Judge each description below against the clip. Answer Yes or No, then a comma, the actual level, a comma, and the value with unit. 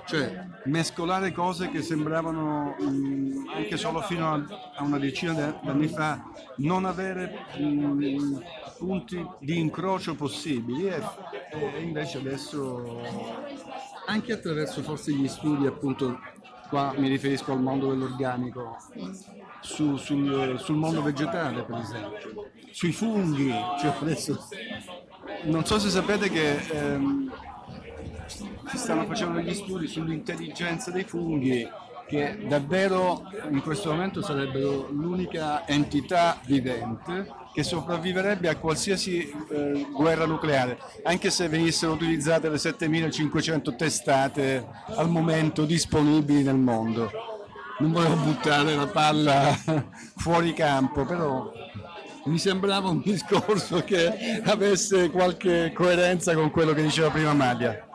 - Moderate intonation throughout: Yes, average, 3.7 semitones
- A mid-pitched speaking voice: Yes, medium, 155 Hz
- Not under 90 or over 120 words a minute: Yes, slow, 115 wpm